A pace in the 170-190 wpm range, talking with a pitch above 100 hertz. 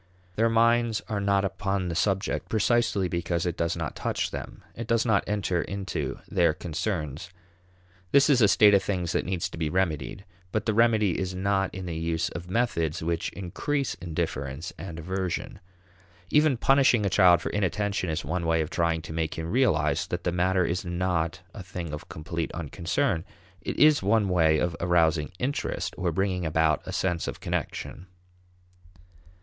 No: average, 175 wpm; very low, 90 Hz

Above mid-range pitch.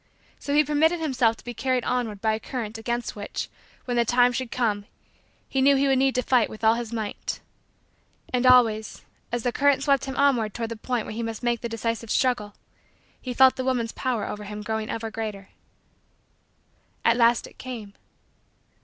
Yes: high, 240 Hz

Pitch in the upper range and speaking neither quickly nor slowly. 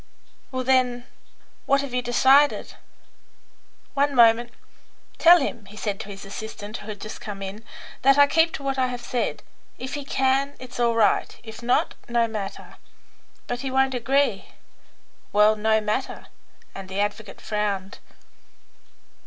Yes: high, 240 Hz; average, 155 wpm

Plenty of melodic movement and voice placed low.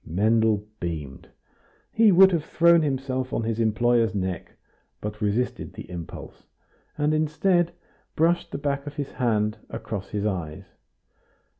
Yes: wide, 6.2 semitones; low, 115 Hz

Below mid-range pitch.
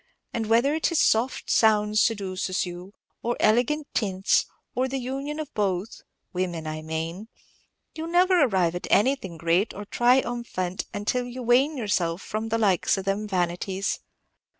No: high, 215 Hz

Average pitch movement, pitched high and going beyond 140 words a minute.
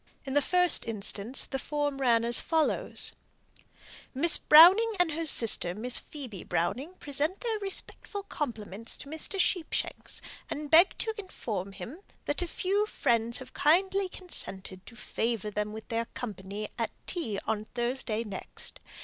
No: wide, 7.6 semitones; very high, 265 Hz; average, 150 wpm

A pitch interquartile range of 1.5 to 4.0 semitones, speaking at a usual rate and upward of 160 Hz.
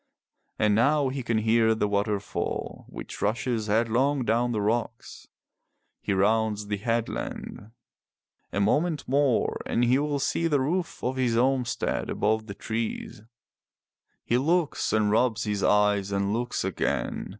No: average, 3.7 semitones; average, 150 wpm; low, 115 Hz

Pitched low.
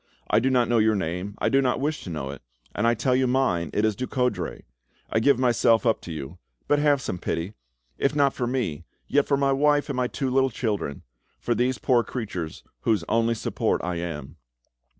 Yes: low, 115 Hz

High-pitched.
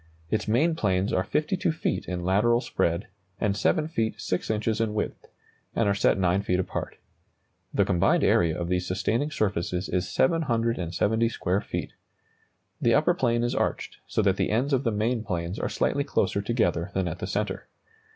No: low, 105 Hz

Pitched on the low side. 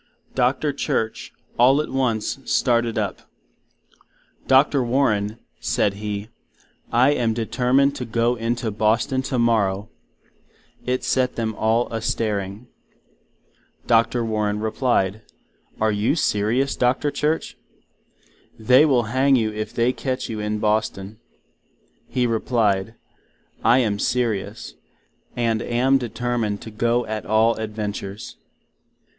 Yes: low, 115 Hz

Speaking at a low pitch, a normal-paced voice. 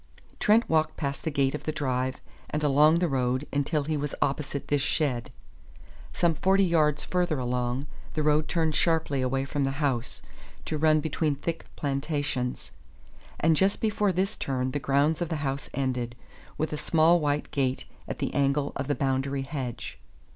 No: medium, 145 Hz; average, 175 wpm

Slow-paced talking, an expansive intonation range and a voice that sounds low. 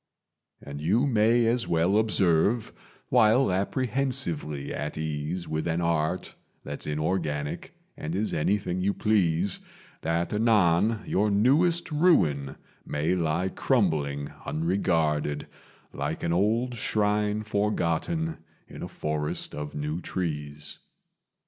Yes: slow, 110 wpm; wide, 5.9 semitones; very low, 90 Hz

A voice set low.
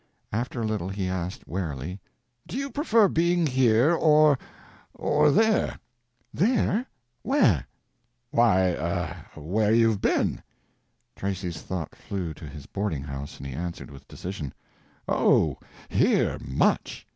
Yes: low, 100 Hz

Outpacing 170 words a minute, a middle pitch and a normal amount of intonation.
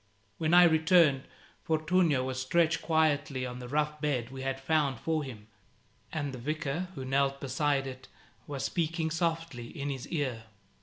No: average, 160 wpm; medium, 145 Hz; average, 3.3 semitones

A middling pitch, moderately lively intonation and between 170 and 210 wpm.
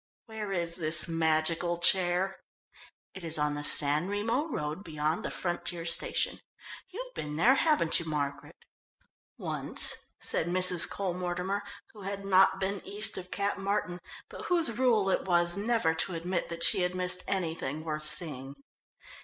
No: medium, 180 Hz; average, 3.5 semitones; average, 155 wpm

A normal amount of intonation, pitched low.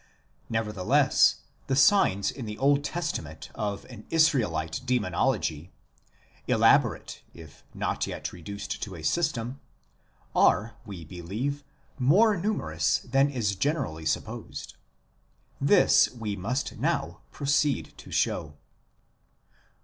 No: wide, 7.7 semitones; low, 110 Hz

